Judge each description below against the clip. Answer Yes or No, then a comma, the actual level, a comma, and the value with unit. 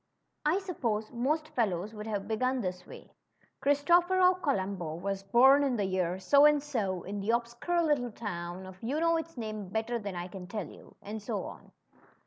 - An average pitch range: No, wide, 6.8 semitones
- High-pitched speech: Yes, high, 220 Hz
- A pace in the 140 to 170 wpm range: No, average, 185 wpm